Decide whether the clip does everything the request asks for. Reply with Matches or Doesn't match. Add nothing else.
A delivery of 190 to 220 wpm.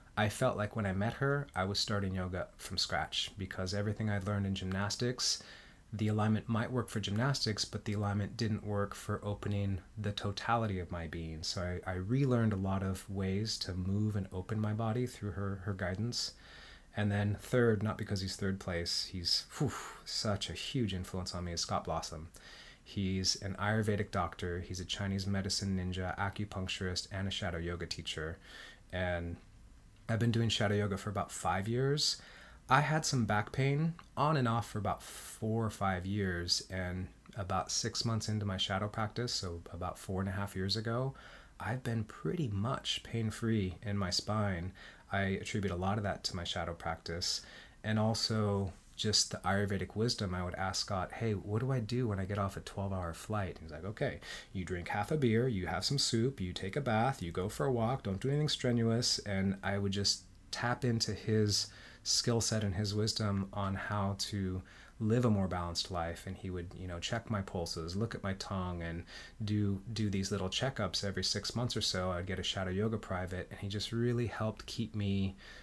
Matches